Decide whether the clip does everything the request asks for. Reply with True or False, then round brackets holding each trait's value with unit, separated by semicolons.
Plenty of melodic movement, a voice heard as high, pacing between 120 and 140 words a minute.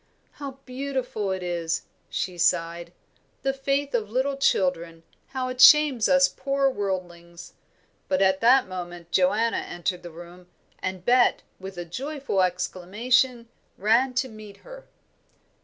True (6.8 semitones; 210 Hz; 135 wpm)